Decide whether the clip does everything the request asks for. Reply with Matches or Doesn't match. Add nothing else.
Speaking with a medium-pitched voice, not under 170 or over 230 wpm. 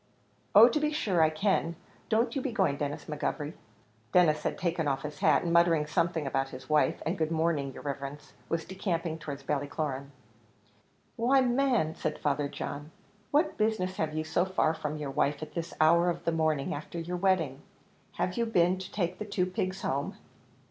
Matches